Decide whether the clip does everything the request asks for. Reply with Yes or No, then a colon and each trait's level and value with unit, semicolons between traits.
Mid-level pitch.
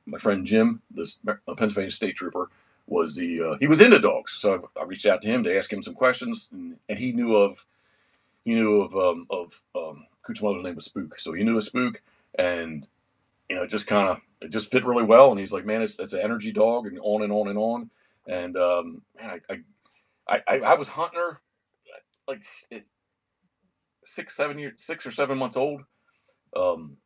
No: low, 120 Hz